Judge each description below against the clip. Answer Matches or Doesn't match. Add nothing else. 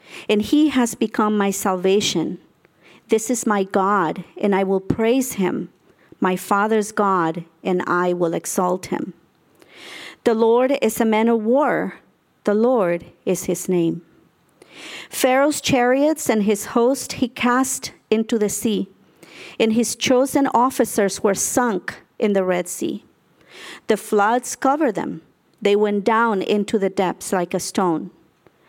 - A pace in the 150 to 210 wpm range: Doesn't match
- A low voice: Doesn't match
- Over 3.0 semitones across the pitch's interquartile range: Matches